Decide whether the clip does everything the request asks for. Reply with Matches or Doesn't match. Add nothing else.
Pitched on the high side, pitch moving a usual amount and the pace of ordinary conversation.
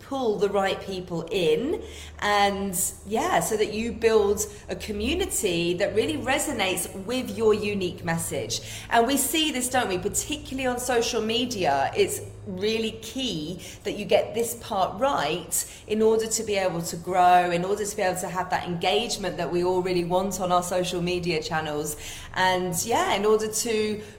Matches